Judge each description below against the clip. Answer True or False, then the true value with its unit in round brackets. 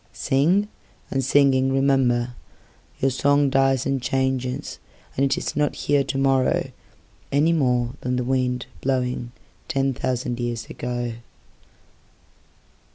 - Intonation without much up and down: True (1.6 semitones)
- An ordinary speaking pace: False (90 wpm)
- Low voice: True (130 Hz)